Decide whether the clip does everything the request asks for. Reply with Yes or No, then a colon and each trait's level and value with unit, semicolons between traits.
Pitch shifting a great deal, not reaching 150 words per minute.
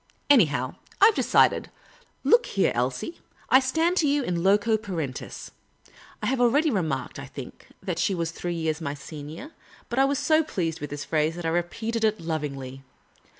No: wide, 8.9 semitones; average, 185 wpm